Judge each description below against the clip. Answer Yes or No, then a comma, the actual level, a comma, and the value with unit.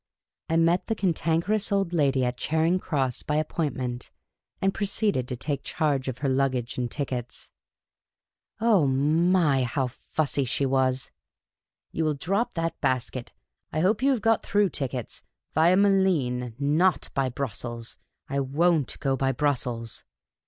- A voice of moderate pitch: Yes, medium, 145 Hz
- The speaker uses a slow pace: No, average, 150 wpm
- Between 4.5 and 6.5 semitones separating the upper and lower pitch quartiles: Yes, average, 5.2 semitones